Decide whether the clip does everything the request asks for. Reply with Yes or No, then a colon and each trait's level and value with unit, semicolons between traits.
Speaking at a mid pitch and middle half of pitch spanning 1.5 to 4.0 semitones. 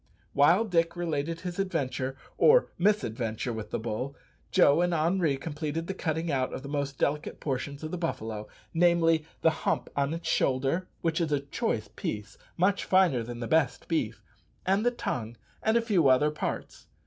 No: medium, 155 Hz; average, 4.7 semitones